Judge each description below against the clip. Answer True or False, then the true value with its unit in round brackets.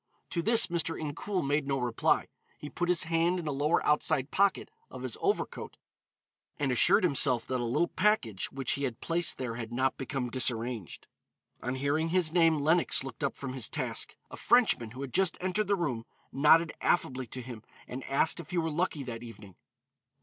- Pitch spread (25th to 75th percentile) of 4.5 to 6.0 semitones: True (5.0 semitones)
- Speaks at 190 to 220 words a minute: True (195 wpm)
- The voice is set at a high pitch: False (145 Hz)